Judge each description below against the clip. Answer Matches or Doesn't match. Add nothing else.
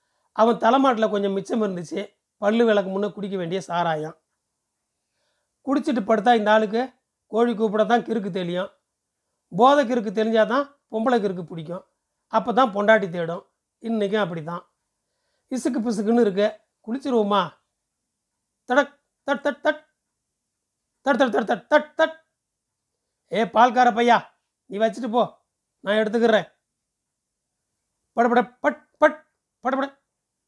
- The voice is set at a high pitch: Matches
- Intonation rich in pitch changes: Doesn't match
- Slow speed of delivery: Doesn't match